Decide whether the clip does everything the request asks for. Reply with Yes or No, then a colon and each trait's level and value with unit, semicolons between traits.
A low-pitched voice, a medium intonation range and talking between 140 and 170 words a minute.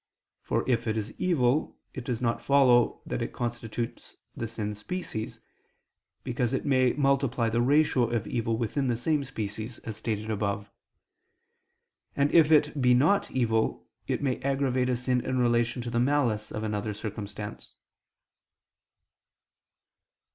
Yes: low, 120 Hz; average, 3.3 semitones; average, 145 wpm